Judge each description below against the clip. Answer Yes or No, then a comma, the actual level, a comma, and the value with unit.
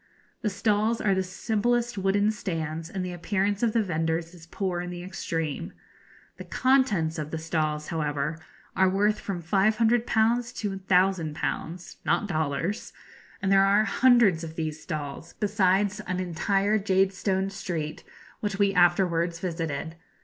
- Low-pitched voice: No, high, 190 Hz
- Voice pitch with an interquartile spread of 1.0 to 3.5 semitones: No, average, 3.9 semitones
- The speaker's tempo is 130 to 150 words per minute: Yes, average, 140 wpm